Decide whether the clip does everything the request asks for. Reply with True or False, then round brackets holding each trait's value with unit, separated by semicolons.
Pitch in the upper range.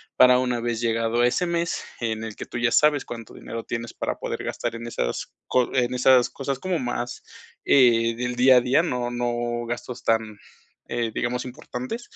False (120 Hz)